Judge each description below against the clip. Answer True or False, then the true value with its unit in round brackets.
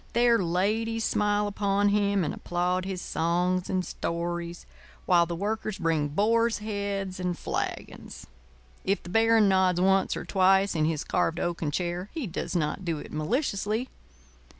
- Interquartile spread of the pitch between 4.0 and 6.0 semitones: False (3.2 semitones)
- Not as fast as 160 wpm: True (150 wpm)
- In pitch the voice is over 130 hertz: True (190 Hz)